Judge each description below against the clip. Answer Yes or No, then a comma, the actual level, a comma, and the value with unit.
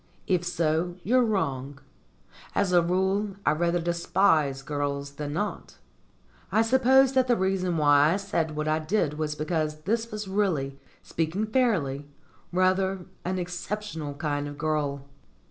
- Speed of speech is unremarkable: Yes, average, 145 wpm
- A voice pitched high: No, medium, 170 Hz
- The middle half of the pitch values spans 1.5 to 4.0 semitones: No, average, 4.7 semitones